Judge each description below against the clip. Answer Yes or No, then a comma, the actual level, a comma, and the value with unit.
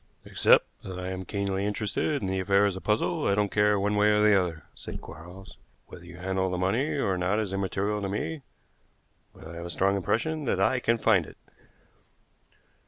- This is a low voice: Yes, low, 100 Hz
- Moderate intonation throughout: No, narrow, 2.0 semitones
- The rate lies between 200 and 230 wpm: Yes, fast, 205 wpm